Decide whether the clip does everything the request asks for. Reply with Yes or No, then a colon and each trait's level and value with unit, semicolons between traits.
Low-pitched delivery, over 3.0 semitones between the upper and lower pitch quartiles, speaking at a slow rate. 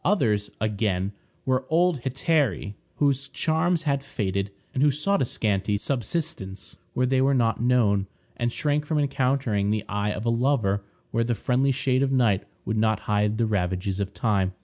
No: low, 120 Hz; average, 5.2 semitones; average, 170 wpm